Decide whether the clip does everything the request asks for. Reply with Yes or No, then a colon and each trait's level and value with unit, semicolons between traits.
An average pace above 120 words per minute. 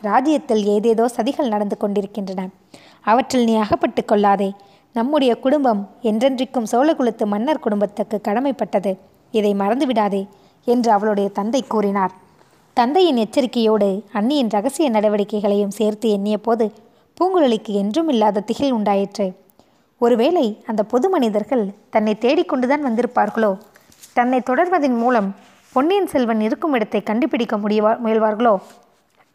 No: average, 105 wpm